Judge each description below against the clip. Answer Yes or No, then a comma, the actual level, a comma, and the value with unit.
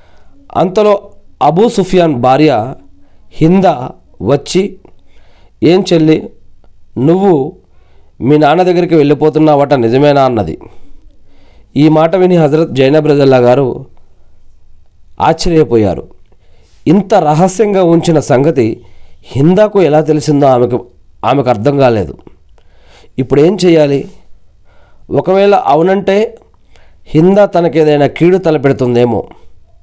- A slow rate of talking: No, average, 85 wpm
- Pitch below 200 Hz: Yes, medium, 140 Hz